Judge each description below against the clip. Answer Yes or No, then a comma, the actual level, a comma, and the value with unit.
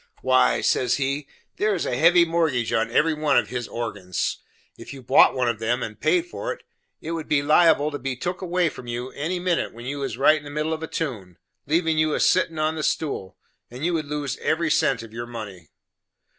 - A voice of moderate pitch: Yes, medium, 145 Hz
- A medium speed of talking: No, fast, 225 wpm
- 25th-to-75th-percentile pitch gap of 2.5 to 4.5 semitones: No, average, 4.9 semitones